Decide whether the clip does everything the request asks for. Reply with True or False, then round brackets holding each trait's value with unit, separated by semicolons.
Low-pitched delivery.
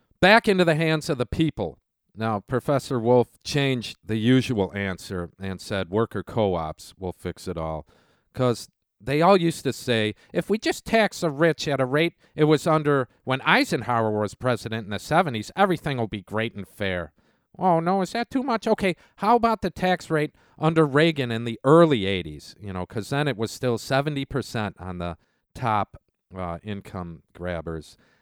True (125 Hz)